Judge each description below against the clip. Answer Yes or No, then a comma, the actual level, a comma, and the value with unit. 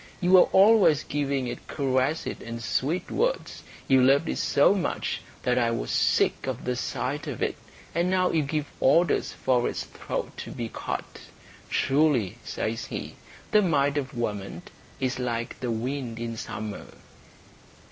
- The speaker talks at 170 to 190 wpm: No, average, 155 wpm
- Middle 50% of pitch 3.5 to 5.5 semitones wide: Yes, average, 4.5 semitones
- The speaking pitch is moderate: No, low, 130 Hz